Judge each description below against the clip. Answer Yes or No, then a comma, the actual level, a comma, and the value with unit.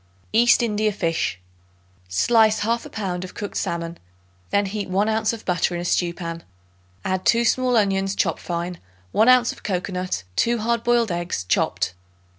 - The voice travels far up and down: No, average, 4.3 semitones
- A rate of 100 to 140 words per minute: No, average, 165 wpm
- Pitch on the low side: No, high, 200 Hz